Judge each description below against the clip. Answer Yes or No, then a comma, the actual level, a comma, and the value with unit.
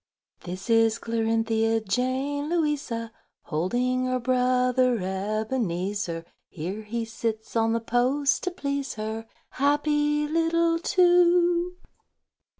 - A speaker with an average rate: No, slow, 105 wpm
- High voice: Yes, high, 245 Hz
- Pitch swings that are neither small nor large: Yes, average, 4.8 semitones